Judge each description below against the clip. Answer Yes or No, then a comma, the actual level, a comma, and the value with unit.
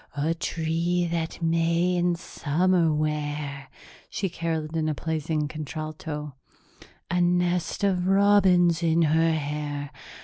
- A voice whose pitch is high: No, medium, 165 Hz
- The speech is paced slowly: Yes, slow, 115 wpm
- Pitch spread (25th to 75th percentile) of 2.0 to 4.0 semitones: Yes, narrow, 2.5 semitones